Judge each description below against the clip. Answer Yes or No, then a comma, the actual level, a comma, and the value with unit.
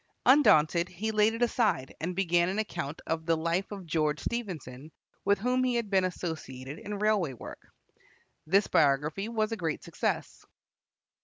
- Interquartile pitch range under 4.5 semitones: No, average, 5.2 semitones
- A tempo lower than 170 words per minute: Yes, average, 160 wpm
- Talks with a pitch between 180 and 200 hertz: Yes, medium, 185 Hz